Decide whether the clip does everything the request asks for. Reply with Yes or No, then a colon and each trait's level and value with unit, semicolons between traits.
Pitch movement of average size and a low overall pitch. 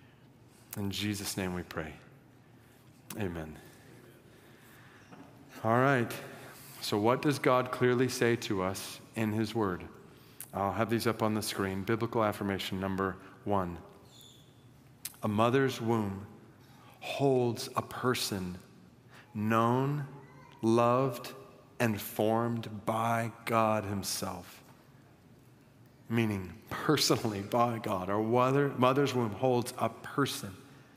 Yes: average, 3.7 semitones; low, 115 Hz